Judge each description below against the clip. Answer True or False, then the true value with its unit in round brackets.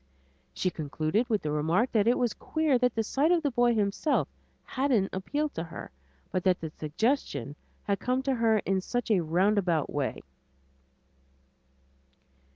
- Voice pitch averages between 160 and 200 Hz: False (210 Hz)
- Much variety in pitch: True (6.6 semitones)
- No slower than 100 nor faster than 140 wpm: False (160 wpm)